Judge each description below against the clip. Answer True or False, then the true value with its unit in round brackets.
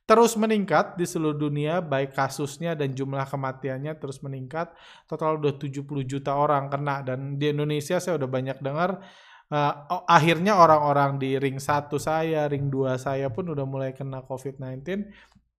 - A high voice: False (145 Hz)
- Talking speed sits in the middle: False (155 wpm)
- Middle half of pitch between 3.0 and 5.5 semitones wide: True (3.4 semitones)